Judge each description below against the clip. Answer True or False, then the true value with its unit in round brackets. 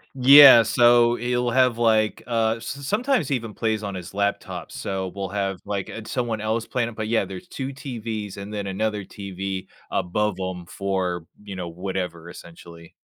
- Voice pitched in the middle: False (105 Hz)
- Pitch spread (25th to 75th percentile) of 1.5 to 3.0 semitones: False (3.6 semitones)